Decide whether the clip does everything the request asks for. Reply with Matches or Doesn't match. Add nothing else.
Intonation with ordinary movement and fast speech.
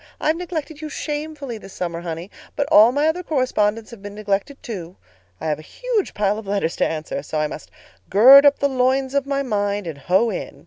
Doesn't match